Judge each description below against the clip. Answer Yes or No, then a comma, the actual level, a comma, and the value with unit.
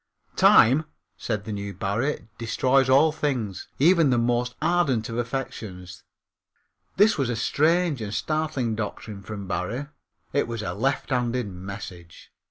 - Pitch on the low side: Yes, low, 120 Hz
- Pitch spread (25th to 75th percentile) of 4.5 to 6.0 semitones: Yes, average, 5.3 semitones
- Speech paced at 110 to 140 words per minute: Yes, slow, 135 wpm